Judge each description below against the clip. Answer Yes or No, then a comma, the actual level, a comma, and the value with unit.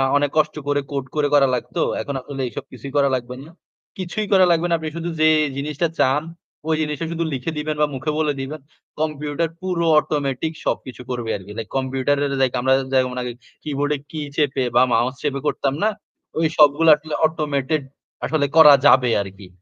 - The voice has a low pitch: No, medium, 145 Hz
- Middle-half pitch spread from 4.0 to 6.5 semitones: No, average, 2.9 semitones